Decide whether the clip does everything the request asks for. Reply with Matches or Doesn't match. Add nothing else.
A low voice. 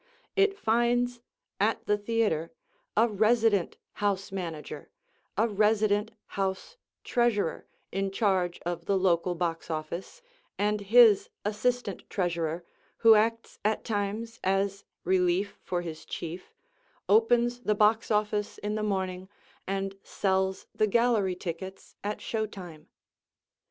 Doesn't match